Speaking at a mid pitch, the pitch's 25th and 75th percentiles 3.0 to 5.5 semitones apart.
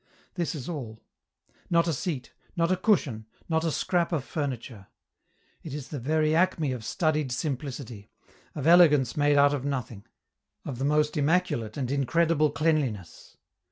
Yes: medium, 145 Hz; average, 4.2 semitones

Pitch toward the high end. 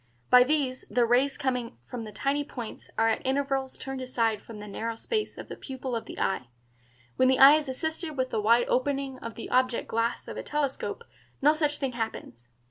Yes: very high, 255 Hz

